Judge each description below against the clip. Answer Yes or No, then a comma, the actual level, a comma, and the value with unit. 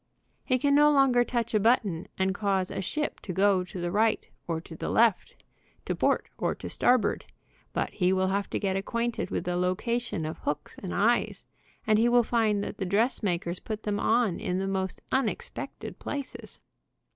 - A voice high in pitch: Yes, high, 205 Hz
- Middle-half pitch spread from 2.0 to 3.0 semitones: No, average, 4.1 semitones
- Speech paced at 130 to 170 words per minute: No, average, 190 wpm